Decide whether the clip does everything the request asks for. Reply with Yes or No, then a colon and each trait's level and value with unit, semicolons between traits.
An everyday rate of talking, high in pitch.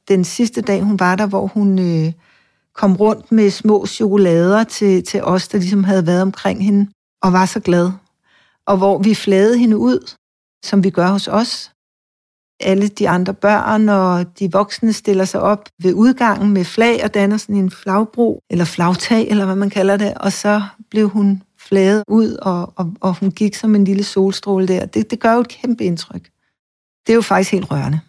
Yes: average, 195 wpm; high, 200 Hz